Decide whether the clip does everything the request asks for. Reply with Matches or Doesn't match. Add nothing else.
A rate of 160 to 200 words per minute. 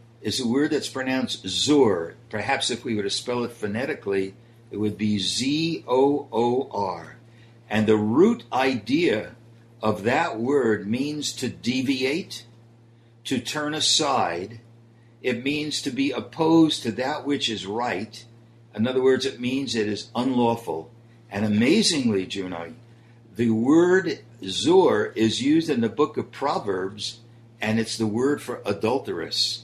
Doesn't match